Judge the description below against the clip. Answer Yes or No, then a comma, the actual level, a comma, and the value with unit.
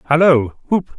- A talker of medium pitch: Yes, medium, 150 Hz